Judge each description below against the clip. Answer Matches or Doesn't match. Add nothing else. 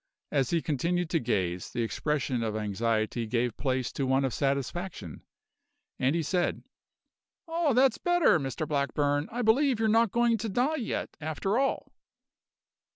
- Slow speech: Doesn't match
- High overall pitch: Doesn't match